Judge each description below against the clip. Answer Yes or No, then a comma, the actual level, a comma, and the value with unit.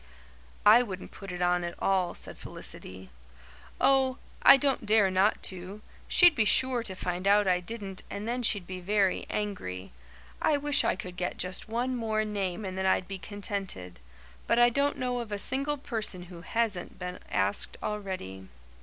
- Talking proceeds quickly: No, average, 180 wpm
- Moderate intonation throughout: Yes, average, 4.3 semitones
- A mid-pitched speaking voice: No, high, 200 Hz